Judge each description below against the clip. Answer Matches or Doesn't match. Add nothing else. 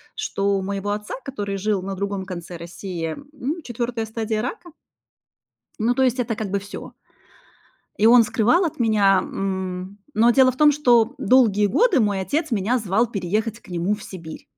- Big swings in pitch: Doesn't match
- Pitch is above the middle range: Matches